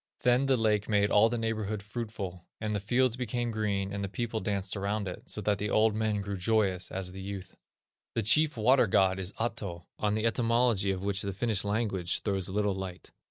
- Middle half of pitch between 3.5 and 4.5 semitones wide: No, narrow, 2.5 semitones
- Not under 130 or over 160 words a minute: No, fast, 205 wpm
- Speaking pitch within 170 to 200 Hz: No, low, 105 Hz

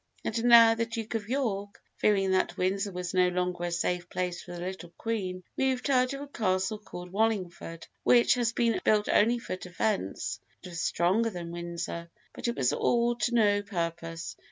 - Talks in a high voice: Yes, high, 195 Hz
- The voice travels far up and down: No, average, 4.4 semitones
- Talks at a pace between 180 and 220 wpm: Yes, average, 185 wpm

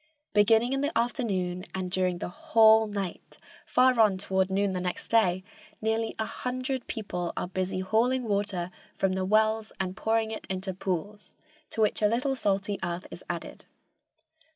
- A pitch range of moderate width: Yes, average, 3.1 semitones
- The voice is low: No, high, 205 Hz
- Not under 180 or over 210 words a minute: No, average, 160 wpm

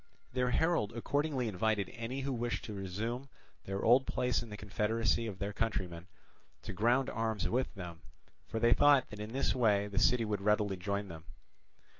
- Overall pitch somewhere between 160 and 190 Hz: No, low, 110 Hz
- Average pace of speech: Yes, average, 180 wpm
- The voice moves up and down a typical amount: Yes, average, 3.6 semitones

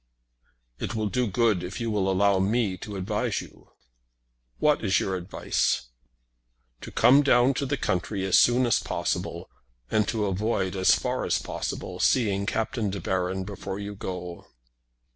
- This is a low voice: Yes, low, 100 Hz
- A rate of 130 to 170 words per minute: Yes, average, 160 wpm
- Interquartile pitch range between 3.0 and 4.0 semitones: Yes, average, 3.5 semitones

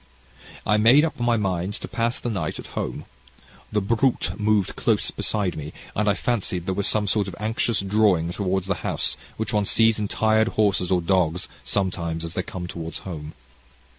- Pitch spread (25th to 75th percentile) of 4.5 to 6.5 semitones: No, average, 3.3 semitones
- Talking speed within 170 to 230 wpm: Yes, average, 190 wpm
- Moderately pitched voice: No, low, 100 Hz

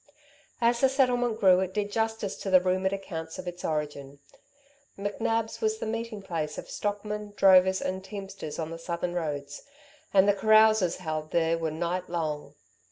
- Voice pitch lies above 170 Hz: Yes, high, 190 Hz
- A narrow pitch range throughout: No, average, 4.2 semitones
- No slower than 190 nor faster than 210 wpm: No, average, 165 wpm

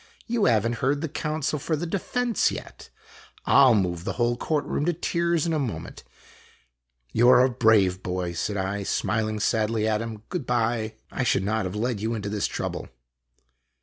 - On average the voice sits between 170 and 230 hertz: No, low, 115 Hz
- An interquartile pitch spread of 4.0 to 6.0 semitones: Yes, wide, 5.6 semitones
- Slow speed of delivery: No, fast, 205 wpm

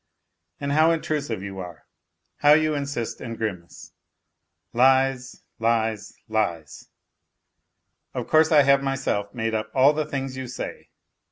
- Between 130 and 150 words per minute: Yes, average, 140 wpm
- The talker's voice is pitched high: No, low, 130 Hz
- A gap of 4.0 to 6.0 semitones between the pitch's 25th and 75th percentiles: Yes, average, 4.6 semitones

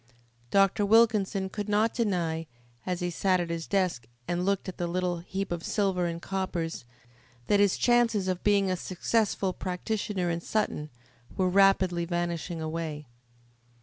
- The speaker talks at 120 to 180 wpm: Yes, average, 150 wpm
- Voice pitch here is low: No, medium, 185 Hz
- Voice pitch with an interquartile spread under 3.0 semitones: Yes, narrow, 2.6 semitones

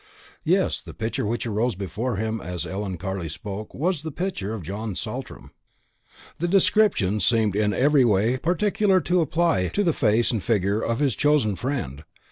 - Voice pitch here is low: Yes, low, 115 Hz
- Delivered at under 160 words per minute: No, average, 170 wpm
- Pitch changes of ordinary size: No, wide, 7.3 semitones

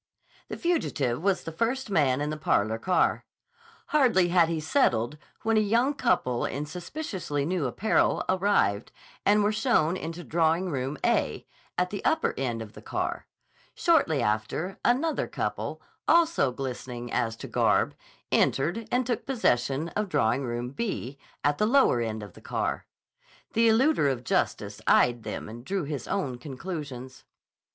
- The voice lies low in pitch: No, medium, 160 Hz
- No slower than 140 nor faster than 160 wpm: Yes, average, 155 wpm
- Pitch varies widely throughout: Yes, wide, 8.9 semitones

